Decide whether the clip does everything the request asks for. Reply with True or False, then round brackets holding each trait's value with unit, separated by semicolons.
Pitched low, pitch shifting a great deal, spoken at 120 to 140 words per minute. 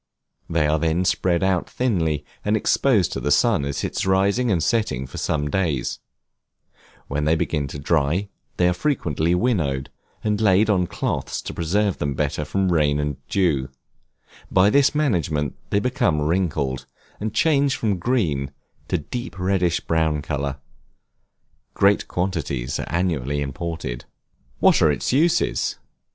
False (85 Hz; 5.7 semitones; 150 wpm)